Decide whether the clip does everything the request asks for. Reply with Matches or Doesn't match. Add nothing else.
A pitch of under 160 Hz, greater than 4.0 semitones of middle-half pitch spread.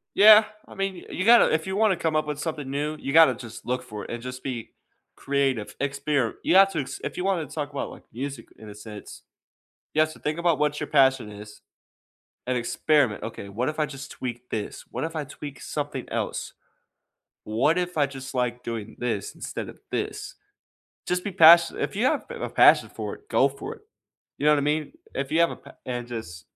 Matches